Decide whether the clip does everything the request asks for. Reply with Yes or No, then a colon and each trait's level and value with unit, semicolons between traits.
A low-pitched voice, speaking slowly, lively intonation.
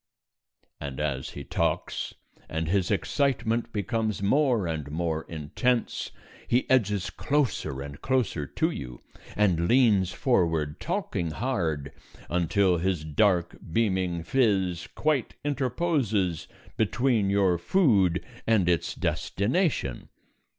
Yes: very low, 95 Hz; slow, 110 wpm; wide, 6.3 semitones